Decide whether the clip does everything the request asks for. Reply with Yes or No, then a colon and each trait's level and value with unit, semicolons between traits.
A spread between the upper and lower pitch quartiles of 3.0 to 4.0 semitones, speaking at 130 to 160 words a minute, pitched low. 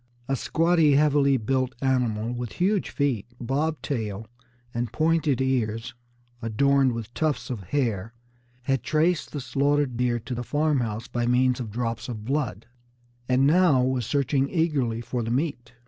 Yes: average, 3.6 semitones; average, 150 wpm; low, 130 Hz